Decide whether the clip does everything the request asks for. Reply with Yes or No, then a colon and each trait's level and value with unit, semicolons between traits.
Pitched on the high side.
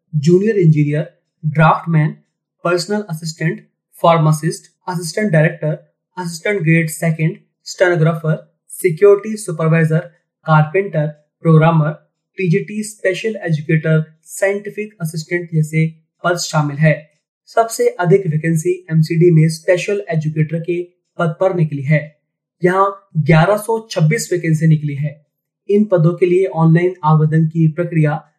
No: medium, 165 Hz